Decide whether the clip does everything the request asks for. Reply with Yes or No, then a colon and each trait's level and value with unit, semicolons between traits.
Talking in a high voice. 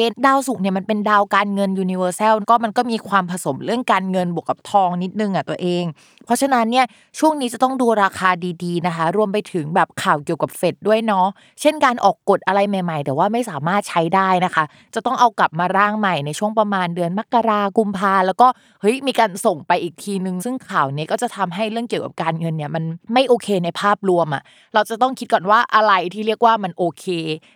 Yes: high, 195 Hz